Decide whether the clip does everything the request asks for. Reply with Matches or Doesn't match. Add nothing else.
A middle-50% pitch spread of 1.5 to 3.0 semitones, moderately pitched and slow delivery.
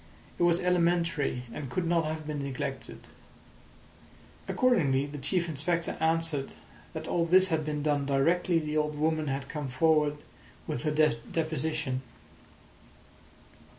Matches